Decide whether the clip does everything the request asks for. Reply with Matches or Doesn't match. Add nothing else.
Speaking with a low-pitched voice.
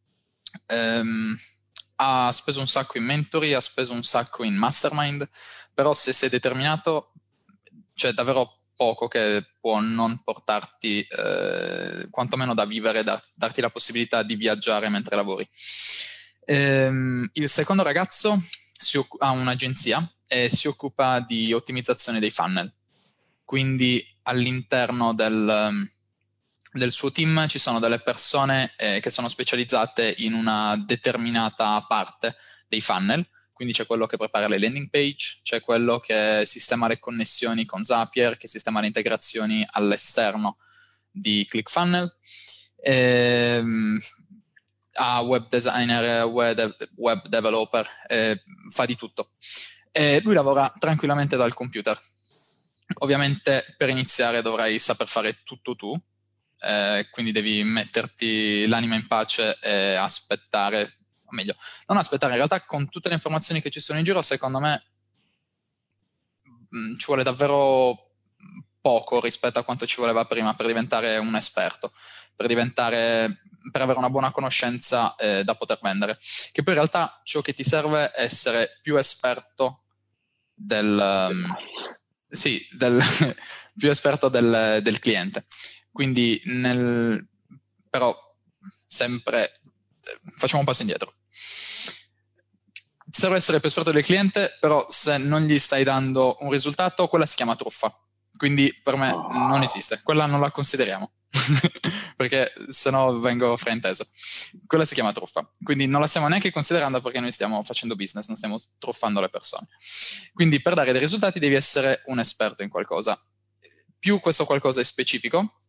Matches